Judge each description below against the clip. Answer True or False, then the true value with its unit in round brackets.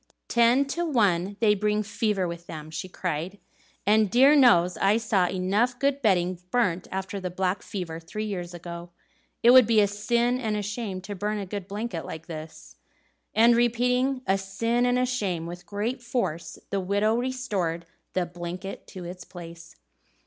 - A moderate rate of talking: True (175 wpm)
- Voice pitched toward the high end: True (200 Hz)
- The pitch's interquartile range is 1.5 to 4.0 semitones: False (4.8 semitones)